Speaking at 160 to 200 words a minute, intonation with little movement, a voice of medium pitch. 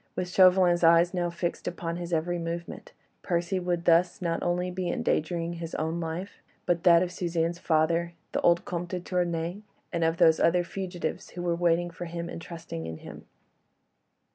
Yes: average, 180 wpm; narrow, 1.0 semitones; medium, 170 Hz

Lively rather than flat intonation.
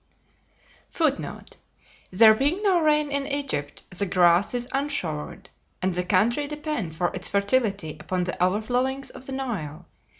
Yes: wide, 7.5 semitones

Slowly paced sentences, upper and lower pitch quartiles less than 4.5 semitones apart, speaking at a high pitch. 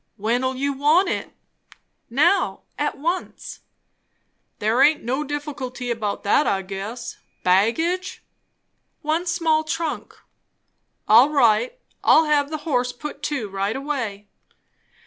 No: slow, 115 wpm; average, 5.2 semitones; very high, 275 Hz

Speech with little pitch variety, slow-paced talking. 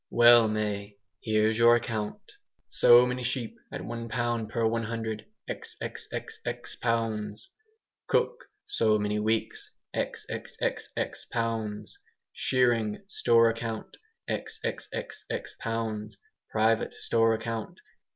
Yes: narrow, 1.5 semitones; slow, 95 wpm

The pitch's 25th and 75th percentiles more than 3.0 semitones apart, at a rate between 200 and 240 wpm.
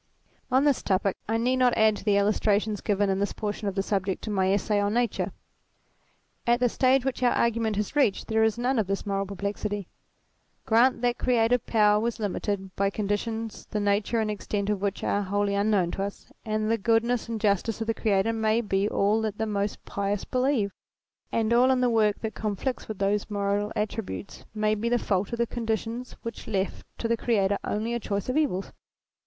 No: narrow, 2.5 semitones; fast, 205 wpm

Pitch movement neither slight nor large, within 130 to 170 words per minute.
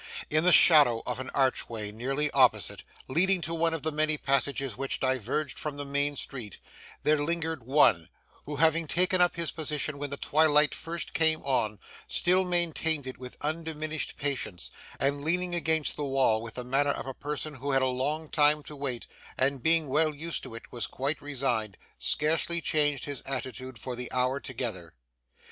No: average, 3.3 semitones; average, 180 wpm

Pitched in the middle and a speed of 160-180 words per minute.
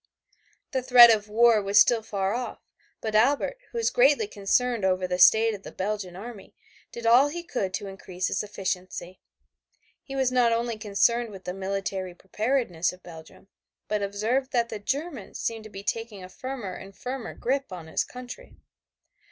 No: high, 215 Hz; average, 175 wpm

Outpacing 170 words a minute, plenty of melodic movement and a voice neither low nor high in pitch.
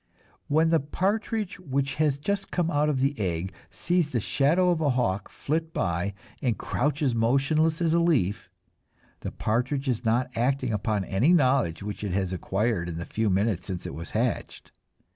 No: average, 180 wpm; wide, 7.4 semitones; low, 130 Hz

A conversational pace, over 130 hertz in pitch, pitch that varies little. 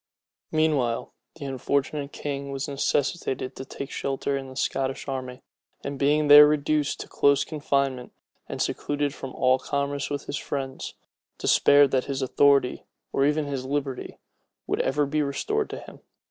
Yes: average, 155 wpm; medium, 140 Hz; narrow, 1.4 semitones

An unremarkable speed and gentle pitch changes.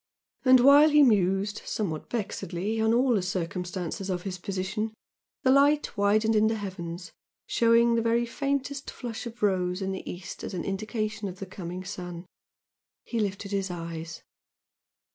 No: average, 160 wpm; average, 4.1 semitones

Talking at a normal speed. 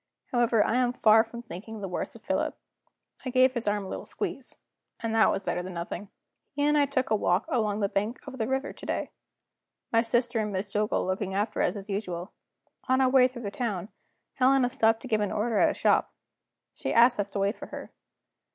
No: fast, 225 wpm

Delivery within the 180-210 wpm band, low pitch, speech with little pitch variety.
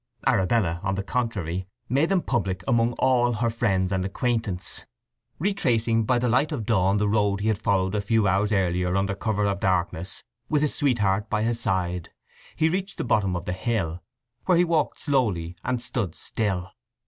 No: average, 185 wpm; low, 105 Hz; average, 4.4 semitones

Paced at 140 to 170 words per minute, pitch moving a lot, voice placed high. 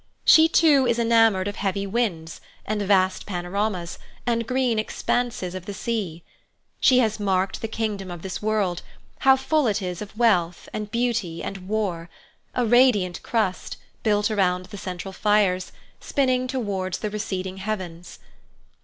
No: average, 145 wpm; average, 3.8 semitones; high, 205 Hz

